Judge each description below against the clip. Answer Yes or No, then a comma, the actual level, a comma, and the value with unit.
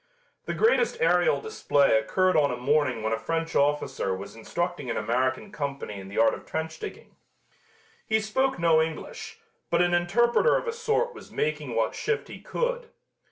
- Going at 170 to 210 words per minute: Yes, average, 175 wpm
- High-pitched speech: No, medium, 160 Hz